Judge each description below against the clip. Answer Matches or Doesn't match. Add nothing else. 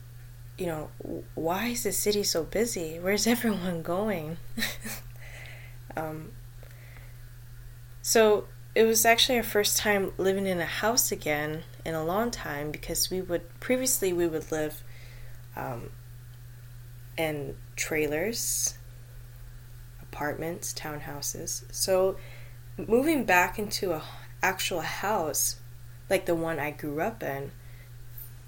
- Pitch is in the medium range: Matches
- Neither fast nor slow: Doesn't match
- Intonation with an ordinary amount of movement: Doesn't match